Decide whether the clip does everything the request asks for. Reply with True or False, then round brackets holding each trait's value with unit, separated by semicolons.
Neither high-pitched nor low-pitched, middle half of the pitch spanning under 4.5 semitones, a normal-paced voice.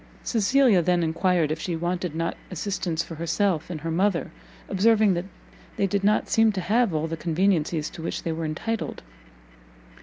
True (175 Hz; 3.6 semitones; 175 wpm)